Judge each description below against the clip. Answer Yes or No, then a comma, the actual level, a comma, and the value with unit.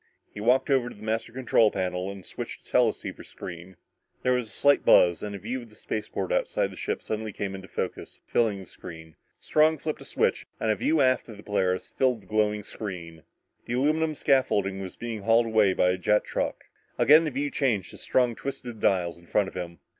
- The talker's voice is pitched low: Yes, low, 110 Hz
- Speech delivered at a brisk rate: Yes, fast, 220 wpm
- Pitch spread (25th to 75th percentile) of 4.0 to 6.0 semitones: Yes, average, 5.2 semitones